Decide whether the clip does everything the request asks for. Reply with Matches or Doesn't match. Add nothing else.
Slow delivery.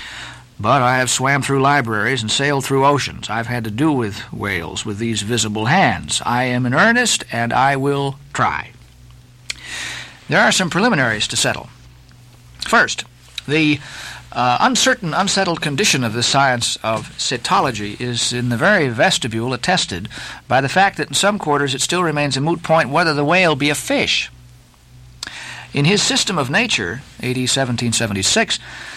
Doesn't match